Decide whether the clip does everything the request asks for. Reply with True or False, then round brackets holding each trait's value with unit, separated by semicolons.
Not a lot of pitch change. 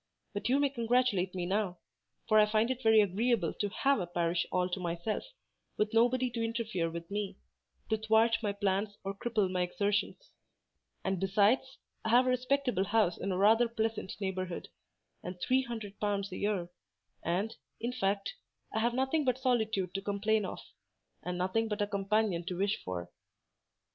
False (3.5 semitones)